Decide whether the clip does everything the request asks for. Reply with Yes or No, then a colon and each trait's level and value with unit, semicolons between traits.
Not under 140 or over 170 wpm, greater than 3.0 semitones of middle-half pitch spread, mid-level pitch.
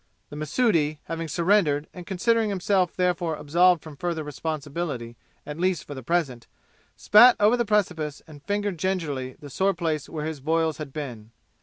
Yes: average, 165 wpm; average, 4.0 semitones; medium, 165 Hz